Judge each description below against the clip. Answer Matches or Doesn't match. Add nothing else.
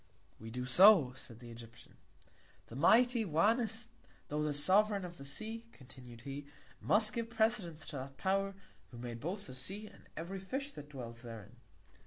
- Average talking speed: Matches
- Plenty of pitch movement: Matches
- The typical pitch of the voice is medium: Matches